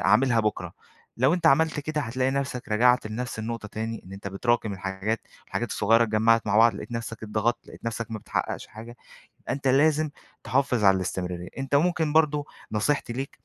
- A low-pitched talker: Yes, low, 115 Hz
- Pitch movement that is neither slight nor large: Yes, average, 4.1 semitones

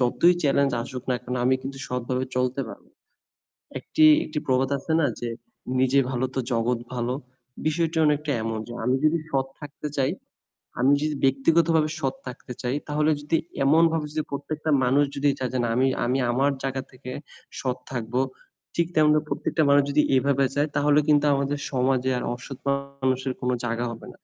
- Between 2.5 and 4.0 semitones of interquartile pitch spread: Yes, average, 2.9 semitones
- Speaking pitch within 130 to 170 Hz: Yes, low, 135 Hz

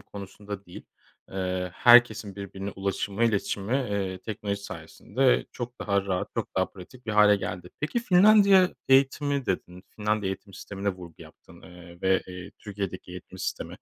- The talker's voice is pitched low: Yes, low, 100 Hz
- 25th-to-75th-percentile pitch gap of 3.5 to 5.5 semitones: Yes, average, 4.3 semitones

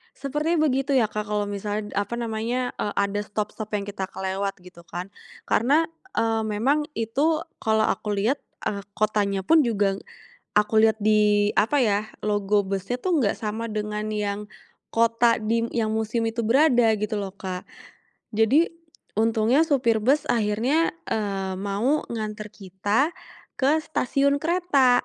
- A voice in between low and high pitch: No, high, 220 Hz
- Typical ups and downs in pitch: Yes, average, 3.5 semitones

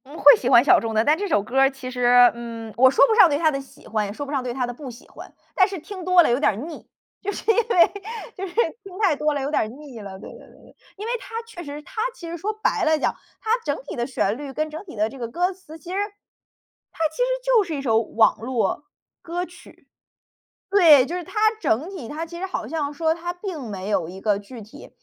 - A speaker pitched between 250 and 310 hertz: Yes, very high, 290 Hz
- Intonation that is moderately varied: No, wide, 6.7 semitones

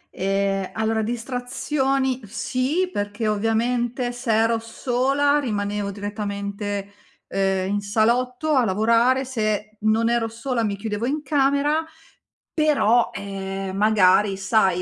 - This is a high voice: Yes, high, 225 Hz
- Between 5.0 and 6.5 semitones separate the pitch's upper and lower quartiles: No, average, 3.7 semitones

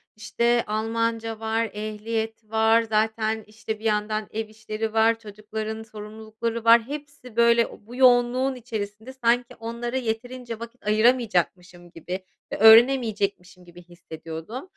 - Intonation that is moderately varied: No, narrow, 1.7 semitones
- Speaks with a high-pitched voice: Yes, high, 220 Hz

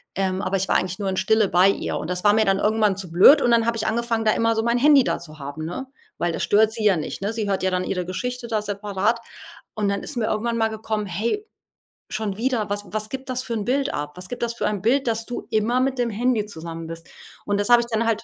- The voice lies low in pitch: No, high, 215 Hz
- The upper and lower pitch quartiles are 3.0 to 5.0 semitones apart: Yes, average, 3.5 semitones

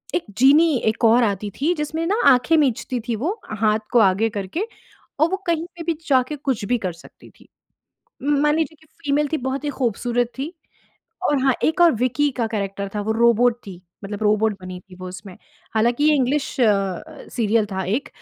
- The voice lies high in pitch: Yes, high, 245 Hz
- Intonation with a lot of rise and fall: Yes, wide, 5.7 semitones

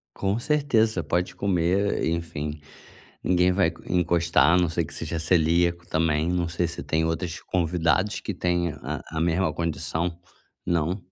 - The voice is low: Yes, very low, 85 Hz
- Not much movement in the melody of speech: Yes, narrow, 1.7 semitones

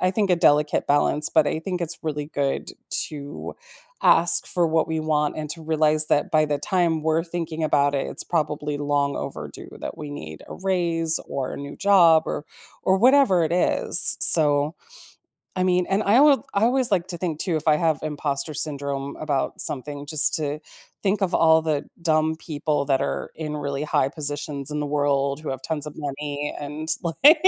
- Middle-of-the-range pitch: Yes, medium, 155 Hz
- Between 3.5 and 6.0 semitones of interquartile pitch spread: No, average, 2.7 semitones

